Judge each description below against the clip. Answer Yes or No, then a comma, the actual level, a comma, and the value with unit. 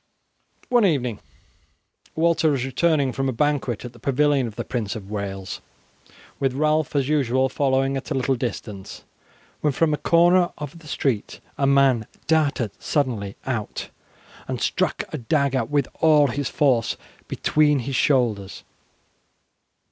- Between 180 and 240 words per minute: No, average, 145 wpm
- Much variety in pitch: No, average, 3.8 semitones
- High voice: No, low, 135 Hz